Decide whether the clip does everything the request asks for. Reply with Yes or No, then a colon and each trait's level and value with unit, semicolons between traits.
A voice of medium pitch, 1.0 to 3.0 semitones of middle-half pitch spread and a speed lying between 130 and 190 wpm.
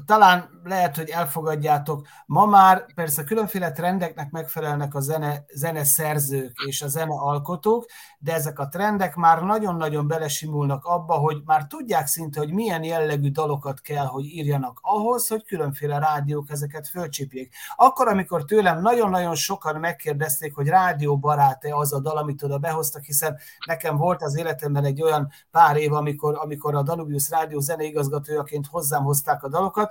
Yes: medium, 155 Hz; narrow, 2.6 semitones; fast, 155 wpm